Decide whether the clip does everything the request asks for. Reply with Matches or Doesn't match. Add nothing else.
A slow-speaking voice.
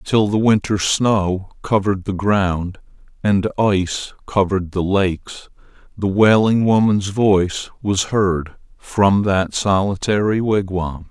Matches